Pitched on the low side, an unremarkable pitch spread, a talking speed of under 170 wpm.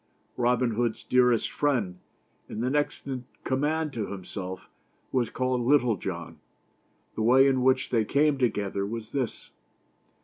Yes: low, 125 Hz; average, 3.2 semitones; average, 140 wpm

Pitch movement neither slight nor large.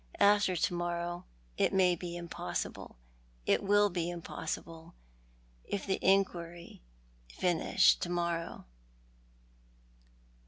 No: narrow, 1.8 semitones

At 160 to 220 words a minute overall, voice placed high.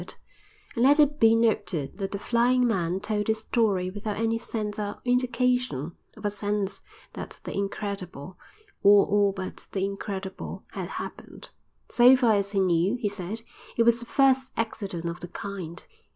Yes: average, 165 wpm; high, 205 Hz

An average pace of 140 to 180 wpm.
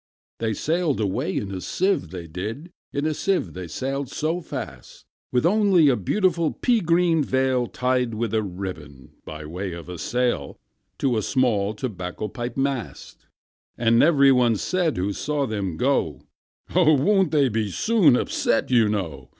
Yes: average, 165 wpm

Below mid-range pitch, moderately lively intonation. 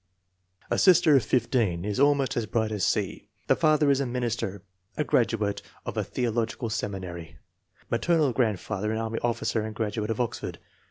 Yes: low, 115 Hz; average, 3.3 semitones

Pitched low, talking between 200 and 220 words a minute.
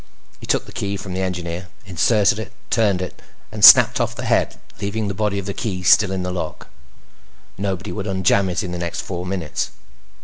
Yes: very low, 95 Hz; fast, 205 wpm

